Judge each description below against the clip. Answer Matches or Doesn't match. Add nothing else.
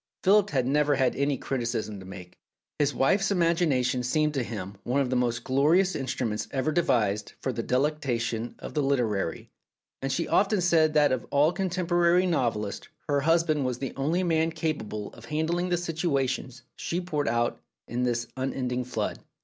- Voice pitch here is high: Doesn't match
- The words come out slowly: Doesn't match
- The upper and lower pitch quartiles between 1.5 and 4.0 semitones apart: Doesn't match